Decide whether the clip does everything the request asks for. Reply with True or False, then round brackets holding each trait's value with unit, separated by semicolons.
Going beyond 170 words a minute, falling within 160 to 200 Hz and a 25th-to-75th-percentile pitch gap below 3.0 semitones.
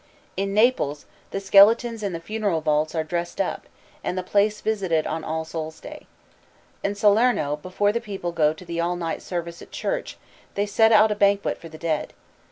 False (190 wpm; 185 Hz; 4.2 semitones)